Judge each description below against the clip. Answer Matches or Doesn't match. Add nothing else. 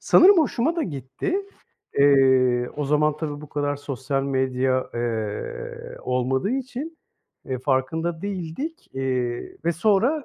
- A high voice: Doesn't match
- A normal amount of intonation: Doesn't match